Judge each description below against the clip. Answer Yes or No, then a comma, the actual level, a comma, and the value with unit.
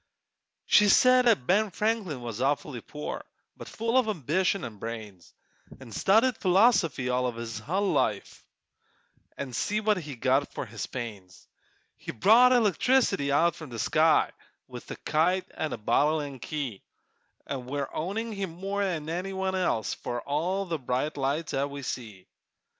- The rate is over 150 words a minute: Yes, average, 160 wpm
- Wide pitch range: Yes, wide, 7.7 semitones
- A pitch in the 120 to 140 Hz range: No, medium, 155 Hz